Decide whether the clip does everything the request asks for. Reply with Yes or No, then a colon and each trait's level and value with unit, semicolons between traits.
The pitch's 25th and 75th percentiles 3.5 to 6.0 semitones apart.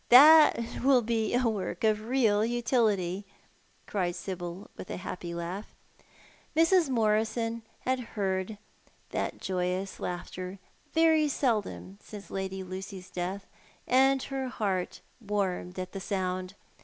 Yes: average, 4.5 semitones